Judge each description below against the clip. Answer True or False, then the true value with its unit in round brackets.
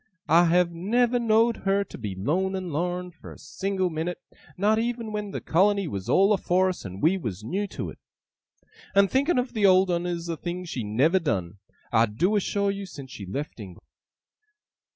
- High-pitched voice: False (180 Hz)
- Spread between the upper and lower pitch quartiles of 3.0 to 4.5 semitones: False (4.9 semitones)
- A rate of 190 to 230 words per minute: True (195 wpm)